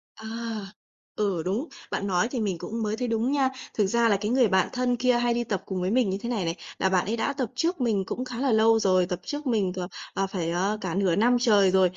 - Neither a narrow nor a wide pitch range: Yes, average, 4.0 semitones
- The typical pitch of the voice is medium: No, high, 215 Hz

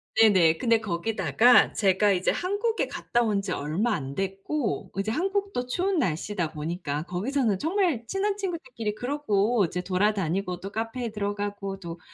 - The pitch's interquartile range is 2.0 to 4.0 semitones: No, wide, 5.4 semitones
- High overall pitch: Yes, high, 210 Hz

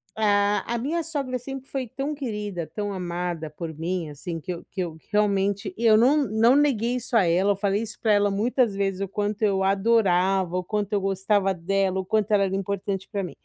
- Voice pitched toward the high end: Yes, high, 200 Hz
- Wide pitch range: No, average, 2.9 semitones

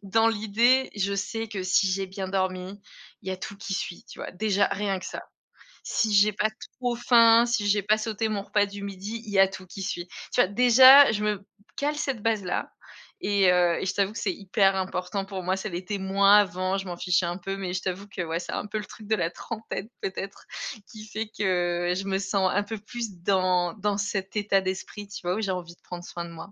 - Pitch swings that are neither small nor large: No, narrow, 2.3 semitones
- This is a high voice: Yes, high, 195 Hz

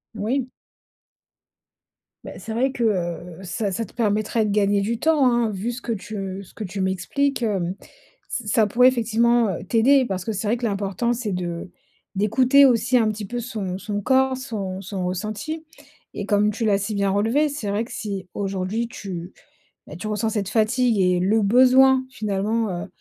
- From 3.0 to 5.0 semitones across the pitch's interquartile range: Yes, average, 3.4 semitones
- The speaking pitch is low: No, high, 215 Hz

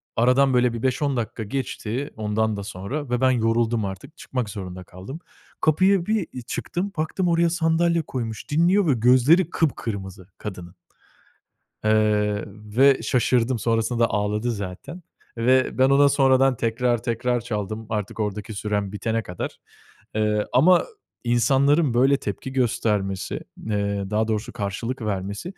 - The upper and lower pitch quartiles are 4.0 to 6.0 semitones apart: Yes, average, 4.3 semitones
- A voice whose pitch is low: Yes, low, 115 Hz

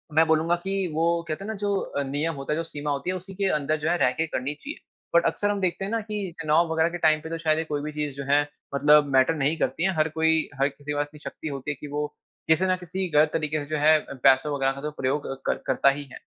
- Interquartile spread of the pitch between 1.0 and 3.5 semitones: Yes, narrow, 2.6 semitones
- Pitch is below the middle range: No, medium, 155 Hz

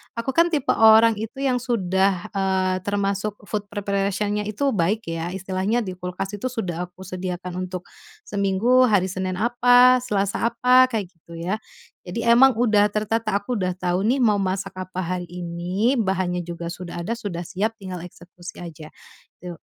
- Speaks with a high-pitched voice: Yes, high, 195 Hz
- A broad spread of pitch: No, average, 3.7 semitones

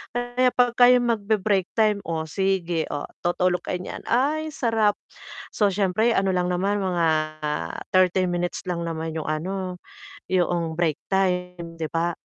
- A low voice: No, medium, 185 Hz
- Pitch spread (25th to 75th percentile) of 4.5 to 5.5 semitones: No, average, 3.4 semitones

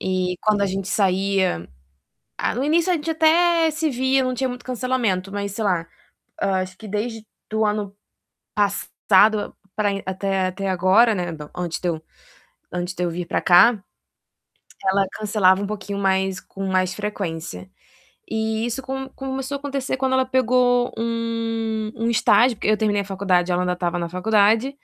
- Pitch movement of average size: Yes, average, 4.6 semitones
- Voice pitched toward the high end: Yes, high, 210 Hz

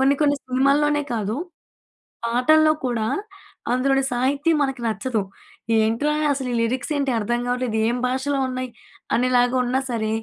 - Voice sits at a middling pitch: No, very high, 255 Hz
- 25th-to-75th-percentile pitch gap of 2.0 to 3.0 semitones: Yes, narrow, 2.5 semitones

